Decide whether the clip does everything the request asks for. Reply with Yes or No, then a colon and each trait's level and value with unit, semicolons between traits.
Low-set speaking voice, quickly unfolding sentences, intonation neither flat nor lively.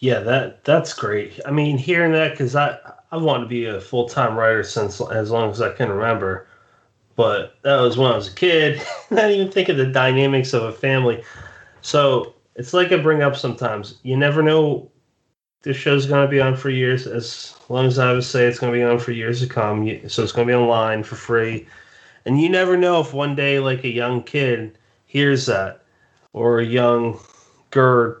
Yes: low, 125 Hz; fast, 210 wpm; average, 3.2 semitones